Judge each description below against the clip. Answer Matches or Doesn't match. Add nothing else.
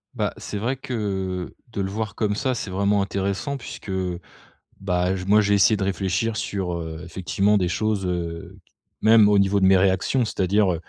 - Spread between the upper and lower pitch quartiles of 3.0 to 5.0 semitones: Doesn't match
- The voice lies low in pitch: Matches